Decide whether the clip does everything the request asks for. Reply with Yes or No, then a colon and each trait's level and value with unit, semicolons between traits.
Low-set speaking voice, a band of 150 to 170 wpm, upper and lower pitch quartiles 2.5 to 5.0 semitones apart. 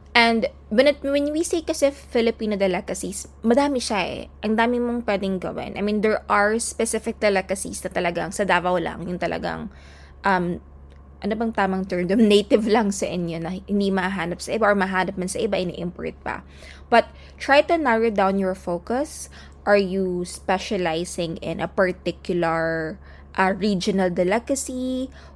No: high, 195 Hz; fast, 155 wpm; average, 4.3 semitones